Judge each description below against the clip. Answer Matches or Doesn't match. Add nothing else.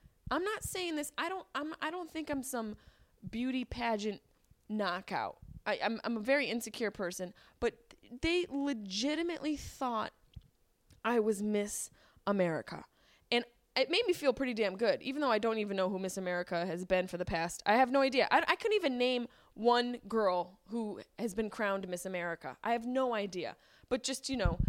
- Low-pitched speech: Doesn't match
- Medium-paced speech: Matches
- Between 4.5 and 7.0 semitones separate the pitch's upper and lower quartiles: Matches